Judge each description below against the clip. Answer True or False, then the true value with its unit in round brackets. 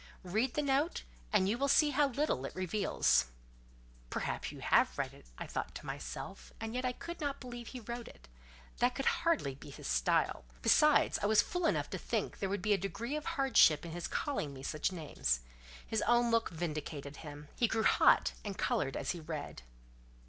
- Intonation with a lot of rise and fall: True (8.9 semitones)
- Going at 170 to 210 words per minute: True (200 wpm)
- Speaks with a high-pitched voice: True (220 Hz)